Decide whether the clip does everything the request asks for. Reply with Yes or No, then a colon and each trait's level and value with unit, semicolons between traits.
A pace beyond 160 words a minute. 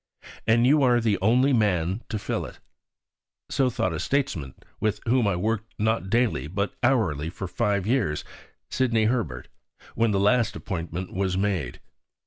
No: average, 155 wpm